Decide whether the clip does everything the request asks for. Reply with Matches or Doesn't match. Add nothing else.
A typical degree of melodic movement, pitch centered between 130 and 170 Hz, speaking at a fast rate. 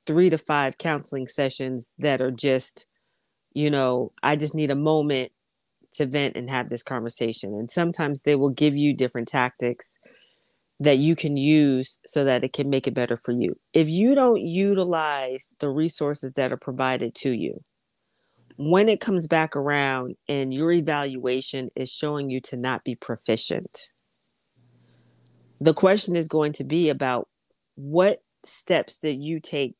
Doesn't match